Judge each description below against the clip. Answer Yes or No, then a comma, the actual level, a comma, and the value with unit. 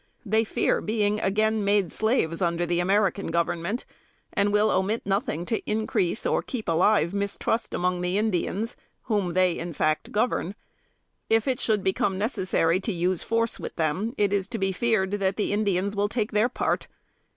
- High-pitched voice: Yes, high, 200 Hz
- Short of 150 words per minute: No, average, 175 wpm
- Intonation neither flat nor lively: Yes, average, 3.1 semitones